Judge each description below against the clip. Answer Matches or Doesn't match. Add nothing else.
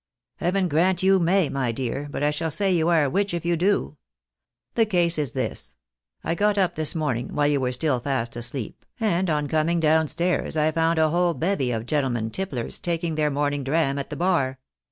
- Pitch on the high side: Doesn't match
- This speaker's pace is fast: Matches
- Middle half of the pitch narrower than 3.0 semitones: Doesn't match